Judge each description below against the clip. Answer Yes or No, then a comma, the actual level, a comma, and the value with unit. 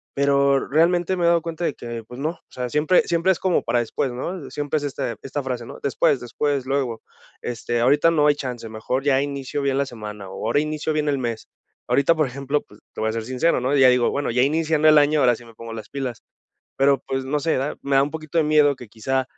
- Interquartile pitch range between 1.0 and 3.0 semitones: No, average, 3.4 semitones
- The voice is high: No, medium, 140 Hz